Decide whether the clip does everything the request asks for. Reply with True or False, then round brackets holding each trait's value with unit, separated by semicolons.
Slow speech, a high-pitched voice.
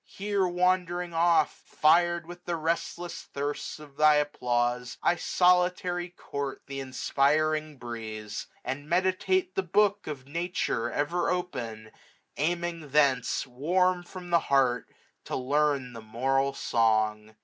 False (125 wpm; 155 Hz)